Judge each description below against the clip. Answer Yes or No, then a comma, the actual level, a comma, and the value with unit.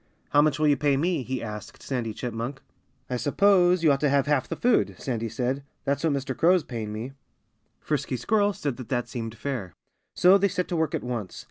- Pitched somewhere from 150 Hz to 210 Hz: No, medium, 140 Hz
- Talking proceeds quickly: Yes, fast, 220 wpm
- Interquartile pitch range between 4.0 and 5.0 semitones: Yes, average, 4.7 semitones